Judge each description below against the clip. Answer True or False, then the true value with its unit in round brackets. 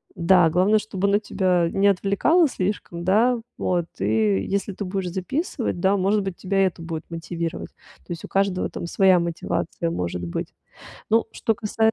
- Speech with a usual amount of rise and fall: True (3.0 semitones)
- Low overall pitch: False (190 Hz)